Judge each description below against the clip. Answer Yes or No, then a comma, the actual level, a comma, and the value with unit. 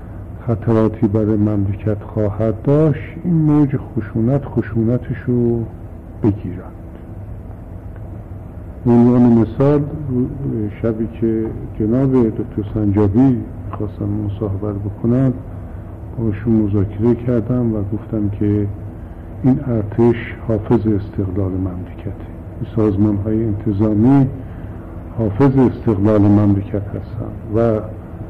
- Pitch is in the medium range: No, low, 110 Hz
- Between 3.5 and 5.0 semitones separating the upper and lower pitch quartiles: No, narrow, 2.4 semitones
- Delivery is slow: Yes, slow, 90 wpm